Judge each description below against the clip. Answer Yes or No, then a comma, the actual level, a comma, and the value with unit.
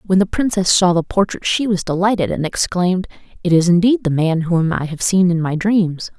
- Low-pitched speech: No, medium, 180 Hz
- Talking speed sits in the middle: No, fast, 225 wpm